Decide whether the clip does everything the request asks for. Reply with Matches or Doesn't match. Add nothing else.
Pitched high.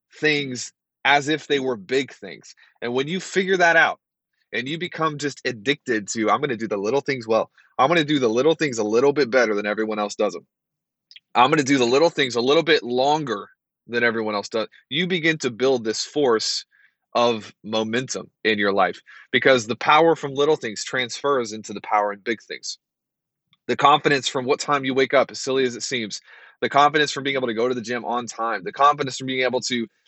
Doesn't match